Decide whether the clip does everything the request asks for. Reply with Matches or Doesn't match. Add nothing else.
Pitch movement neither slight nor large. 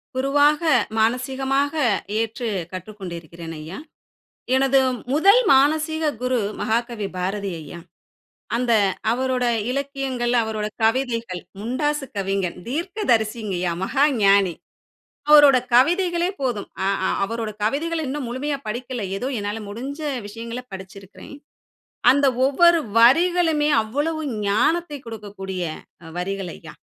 Doesn't match